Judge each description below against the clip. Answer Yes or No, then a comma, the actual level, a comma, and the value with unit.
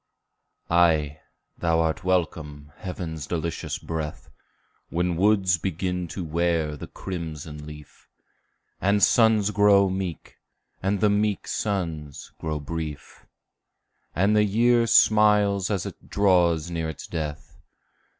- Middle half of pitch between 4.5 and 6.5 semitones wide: No, average, 4.0 semitones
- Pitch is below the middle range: Yes, very low, 85 Hz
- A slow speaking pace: Yes, slow, 115 wpm